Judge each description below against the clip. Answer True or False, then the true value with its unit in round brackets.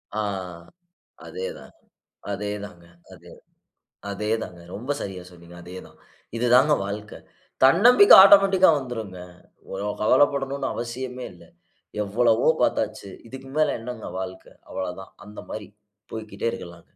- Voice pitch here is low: True (110 Hz)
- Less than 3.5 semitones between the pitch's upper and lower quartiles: False (5.2 semitones)